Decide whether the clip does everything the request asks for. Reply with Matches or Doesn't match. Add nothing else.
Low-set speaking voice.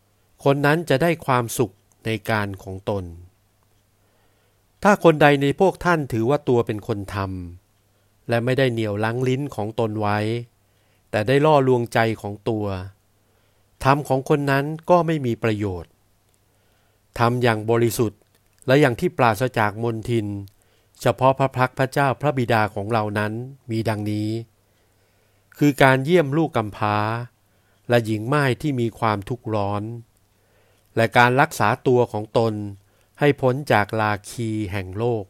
Matches